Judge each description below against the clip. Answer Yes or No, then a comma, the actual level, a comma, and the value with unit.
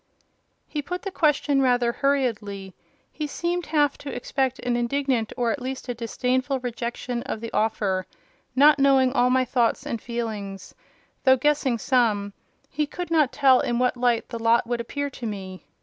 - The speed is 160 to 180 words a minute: Yes, average, 170 wpm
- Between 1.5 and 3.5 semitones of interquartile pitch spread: Yes, average, 3.2 semitones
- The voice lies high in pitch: Yes, very high, 250 Hz